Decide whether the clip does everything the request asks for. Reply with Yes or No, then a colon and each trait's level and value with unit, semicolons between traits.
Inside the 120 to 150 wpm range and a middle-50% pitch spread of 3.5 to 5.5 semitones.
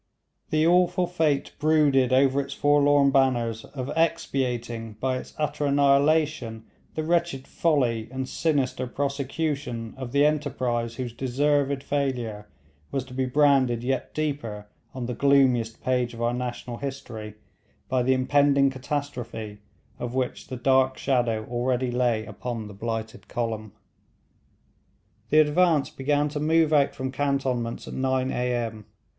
No: slow, 135 wpm; average, 3.1 semitones